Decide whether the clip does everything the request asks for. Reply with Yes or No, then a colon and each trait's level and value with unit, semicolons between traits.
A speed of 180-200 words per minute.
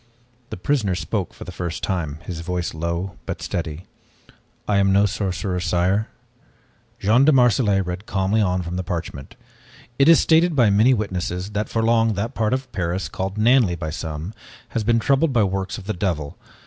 Yes: average, 185 wpm